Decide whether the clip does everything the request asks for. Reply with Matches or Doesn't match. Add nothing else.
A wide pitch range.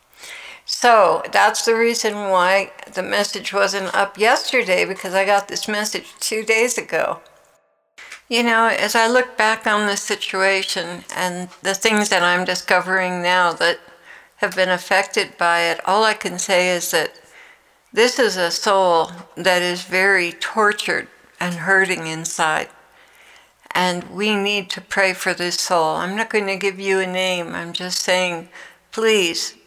Doesn't match